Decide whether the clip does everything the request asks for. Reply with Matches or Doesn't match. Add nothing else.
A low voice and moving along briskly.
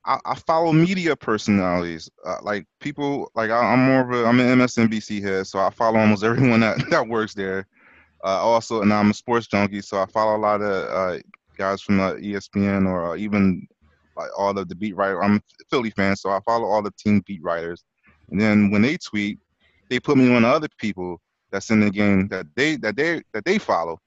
Matches